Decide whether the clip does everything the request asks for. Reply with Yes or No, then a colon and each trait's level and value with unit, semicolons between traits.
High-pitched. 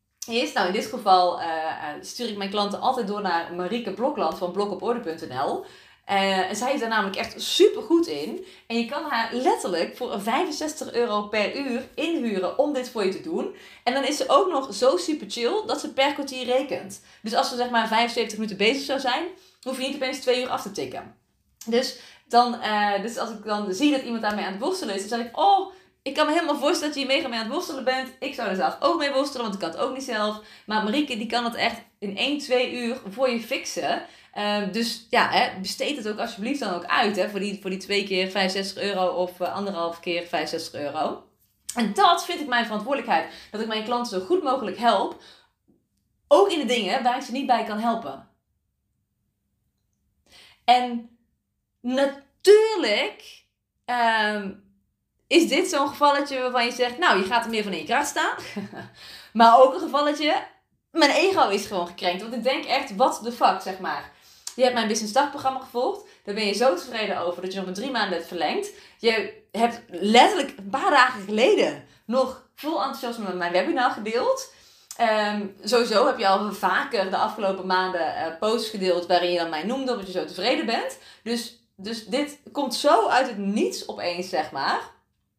Yes: high, 235 Hz